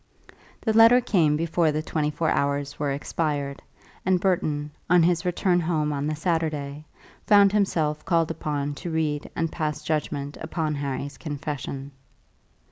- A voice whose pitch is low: No, medium, 155 Hz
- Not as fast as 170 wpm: Yes, average, 145 wpm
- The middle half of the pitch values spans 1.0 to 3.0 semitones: Yes, narrow, 2.6 semitones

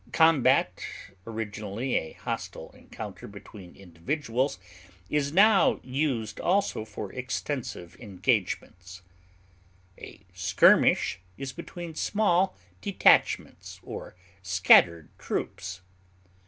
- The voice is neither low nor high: No, low, 120 Hz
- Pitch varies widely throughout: Yes, wide, 8.6 semitones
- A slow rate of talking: Yes, slow, 85 wpm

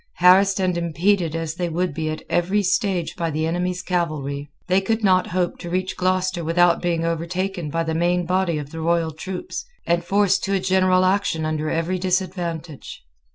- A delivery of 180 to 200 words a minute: Yes, average, 185 wpm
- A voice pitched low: No, medium, 175 Hz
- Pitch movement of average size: No, narrow, 2.2 semitones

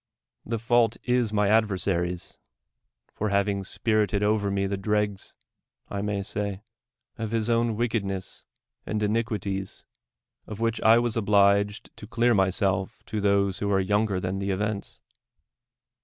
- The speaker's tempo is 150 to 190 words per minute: No, average, 140 wpm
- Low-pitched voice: Yes, low, 105 Hz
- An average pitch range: No, narrow, 2.0 semitones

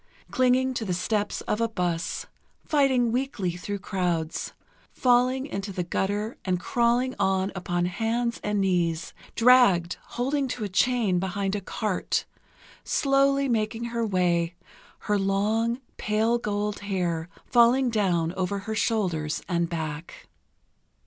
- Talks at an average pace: No, slow, 130 wpm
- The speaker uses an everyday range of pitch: Yes, average, 4.8 semitones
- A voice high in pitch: Yes, high, 205 Hz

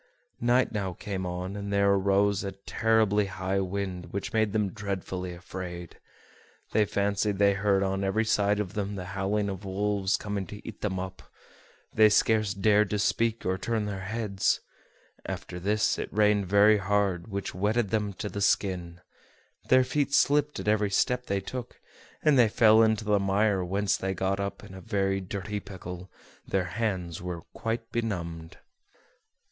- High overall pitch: No, low, 100 Hz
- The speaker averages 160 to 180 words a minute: Yes, average, 170 wpm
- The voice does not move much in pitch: Yes, narrow, 1.9 semitones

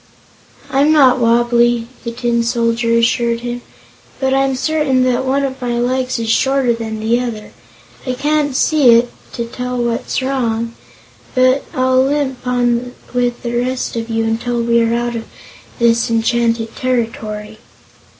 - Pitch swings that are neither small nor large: No, narrow, 1.8 semitones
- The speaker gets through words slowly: No, average, 155 wpm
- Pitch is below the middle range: No, high, 240 Hz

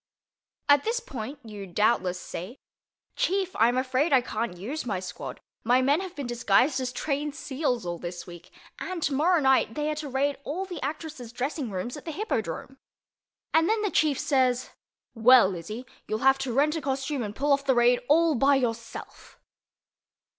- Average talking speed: Yes, average, 180 wpm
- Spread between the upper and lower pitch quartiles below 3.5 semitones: No, average, 4.6 semitones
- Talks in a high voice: Yes, very high, 265 Hz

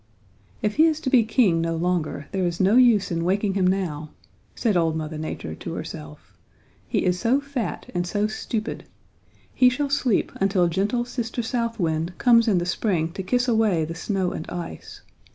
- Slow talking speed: No, average, 190 wpm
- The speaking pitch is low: No, high, 195 Hz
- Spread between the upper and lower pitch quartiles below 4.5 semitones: No, wide, 5.4 semitones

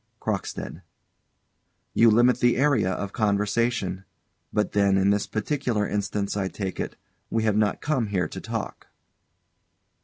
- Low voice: Yes, low, 105 Hz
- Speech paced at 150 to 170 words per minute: No, average, 140 wpm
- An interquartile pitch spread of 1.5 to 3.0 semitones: Yes, average, 2.7 semitones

